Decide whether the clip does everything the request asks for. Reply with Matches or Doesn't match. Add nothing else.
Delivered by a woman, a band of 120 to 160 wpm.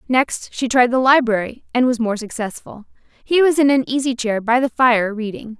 Doesn't match